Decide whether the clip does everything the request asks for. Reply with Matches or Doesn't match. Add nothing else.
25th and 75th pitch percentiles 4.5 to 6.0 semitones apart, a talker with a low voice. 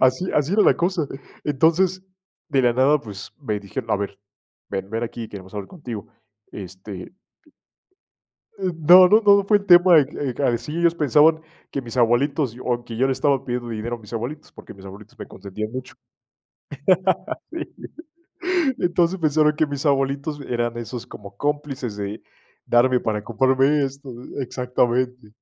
Matches